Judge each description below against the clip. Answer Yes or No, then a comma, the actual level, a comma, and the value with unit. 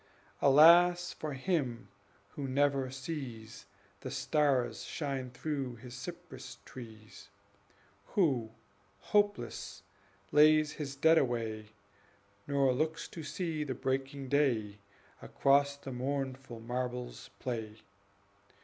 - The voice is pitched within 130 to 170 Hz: Yes, low, 135 Hz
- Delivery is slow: Yes, slow, 100 wpm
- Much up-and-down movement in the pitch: No, average, 3.5 semitones